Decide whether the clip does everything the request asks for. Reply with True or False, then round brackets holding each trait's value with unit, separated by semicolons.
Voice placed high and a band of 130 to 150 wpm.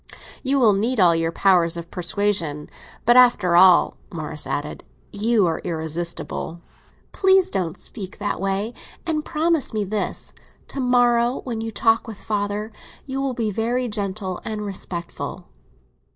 True (205 Hz; 140 wpm)